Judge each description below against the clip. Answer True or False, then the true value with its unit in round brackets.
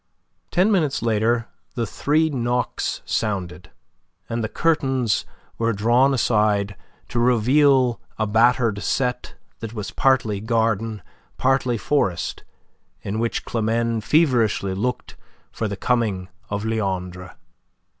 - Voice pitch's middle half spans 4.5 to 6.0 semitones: False (3.1 semitones)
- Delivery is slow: True (115 wpm)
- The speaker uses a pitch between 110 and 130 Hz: True (115 Hz)